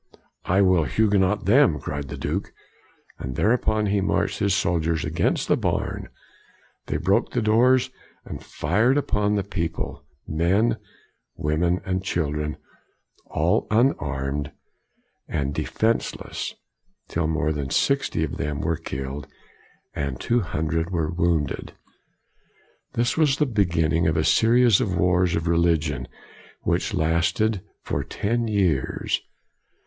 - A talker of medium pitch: No, very low, 85 Hz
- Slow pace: Yes, slow, 130 wpm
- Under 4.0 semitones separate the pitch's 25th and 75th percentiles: No, wide, 5.5 semitones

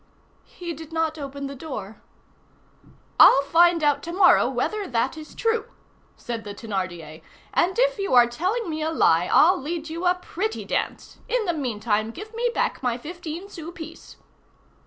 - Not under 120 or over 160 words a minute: No, average, 170 wpm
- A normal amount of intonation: No, wide, 6.5 semitones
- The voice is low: No, very high, 320 Hz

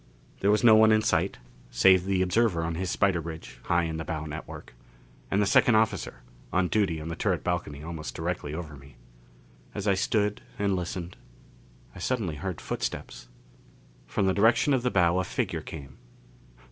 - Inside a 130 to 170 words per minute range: No, average, 180 wpm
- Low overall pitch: Yes, very low, 90 Hz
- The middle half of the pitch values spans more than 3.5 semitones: Yes, average, 3.9 semitones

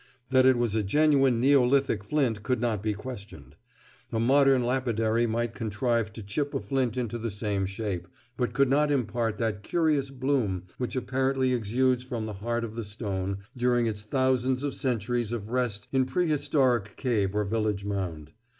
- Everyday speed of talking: Yes, average, 170 wpm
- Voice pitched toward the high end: No, low, 120 Hz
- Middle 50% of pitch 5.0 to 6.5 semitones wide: No, average, 3.8 semitones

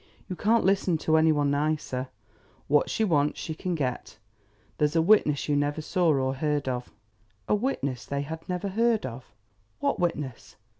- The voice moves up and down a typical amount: Yes, average, 4.2 semitones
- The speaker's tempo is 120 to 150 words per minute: No, average, 170 wpm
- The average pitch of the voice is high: No, medium, 155 Hz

